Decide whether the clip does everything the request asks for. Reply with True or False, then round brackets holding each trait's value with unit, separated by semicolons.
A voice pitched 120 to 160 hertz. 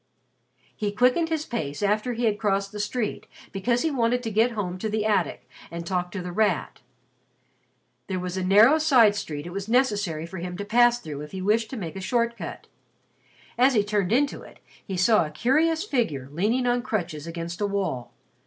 False (210 Hz)